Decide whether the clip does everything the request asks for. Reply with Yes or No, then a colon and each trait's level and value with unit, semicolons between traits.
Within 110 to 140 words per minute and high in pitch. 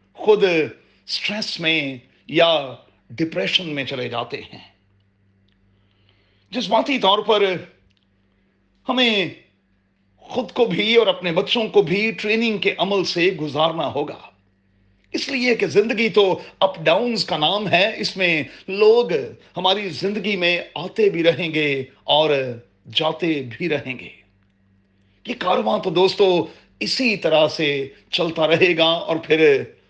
No: average, 130 wpm; medium, 170 Hz